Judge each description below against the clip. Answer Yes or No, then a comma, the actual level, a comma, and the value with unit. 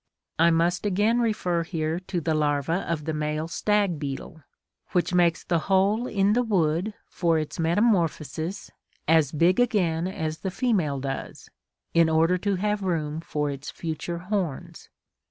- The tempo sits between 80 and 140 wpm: No, average, 155 wpm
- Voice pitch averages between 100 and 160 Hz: No, medium, 170 Hz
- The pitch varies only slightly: No, average, 3.6 semitones